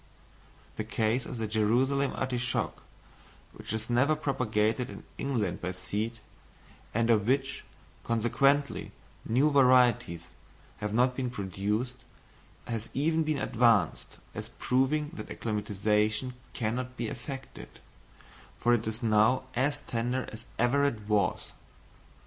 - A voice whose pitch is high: No, low, 120 Hz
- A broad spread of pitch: No, average, 3.4 semitones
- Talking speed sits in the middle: No, slow, 120 wpm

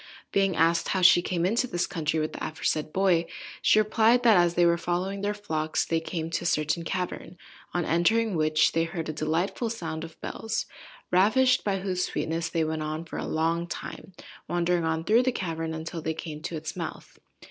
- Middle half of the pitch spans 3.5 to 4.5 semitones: No, average, 3.0 semitones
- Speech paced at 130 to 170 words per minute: No, average, 200 wpm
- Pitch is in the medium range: Yes, medium, 170 Hz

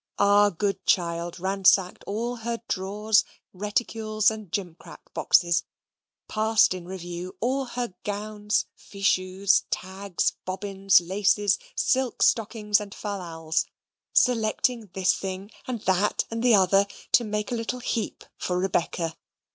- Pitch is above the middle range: Yes, high, 200 Hz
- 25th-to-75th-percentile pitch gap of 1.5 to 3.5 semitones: Yes, average, 2.7 semitones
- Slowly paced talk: Yes, slow, 125 wpm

